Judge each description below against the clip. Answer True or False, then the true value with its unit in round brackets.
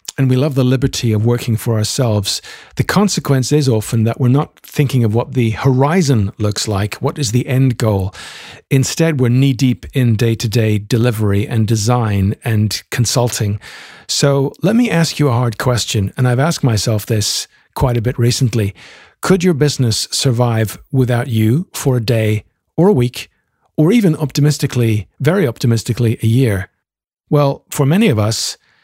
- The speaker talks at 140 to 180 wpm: True (170 wpm)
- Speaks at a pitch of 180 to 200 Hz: False (125 Hz)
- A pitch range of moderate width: True (3.9 semitones)